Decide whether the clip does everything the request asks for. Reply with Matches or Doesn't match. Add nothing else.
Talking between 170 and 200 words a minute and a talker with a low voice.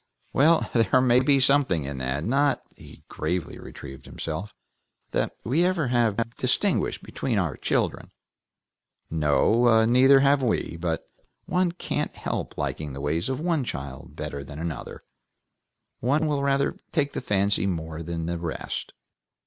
Doesn't match